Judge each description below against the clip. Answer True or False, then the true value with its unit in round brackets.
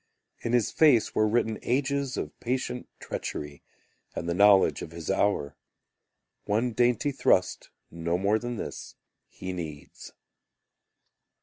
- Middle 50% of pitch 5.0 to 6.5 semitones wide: True (5.5 semitones)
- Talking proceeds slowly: True (125 wpm)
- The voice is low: True (110 Hz)